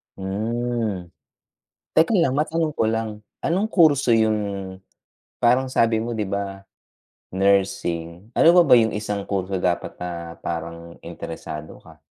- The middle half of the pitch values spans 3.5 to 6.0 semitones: Yes, average, 4.3 semitones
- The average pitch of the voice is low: Yes, low, 105 Hz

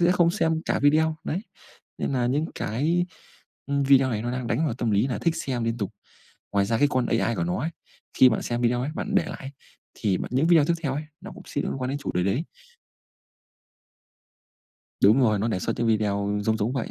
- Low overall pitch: Yes, low, 130 Hz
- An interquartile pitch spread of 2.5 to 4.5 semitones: No, wide, 5.6 semitones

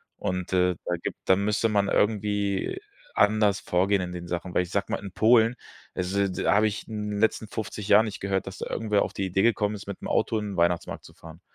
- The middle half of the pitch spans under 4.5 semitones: Yes, narrow, 2.5 semitones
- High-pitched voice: No, low, 100 Hz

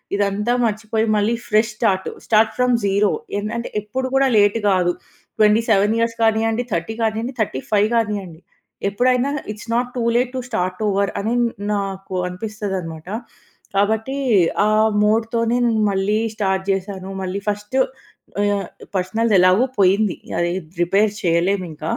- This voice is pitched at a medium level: No, high, 210 Hz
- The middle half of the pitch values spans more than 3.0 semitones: No, average, 2.7 semitones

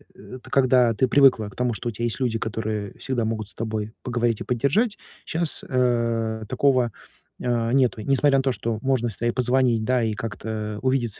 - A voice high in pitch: No, low, 120 Hz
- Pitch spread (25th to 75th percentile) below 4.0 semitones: Yes, narrow, 2.6 semitones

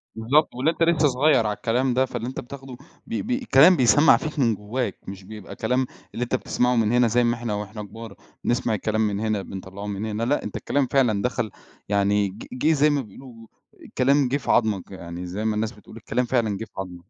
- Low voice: Yes, low, 115 Hz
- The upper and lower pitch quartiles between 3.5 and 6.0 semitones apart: Yes, average, 3.9 semitones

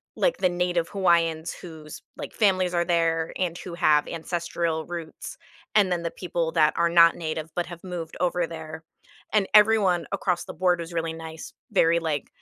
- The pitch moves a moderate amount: No, narrow, 1.6 semitones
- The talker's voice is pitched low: No, medium, 170 Hz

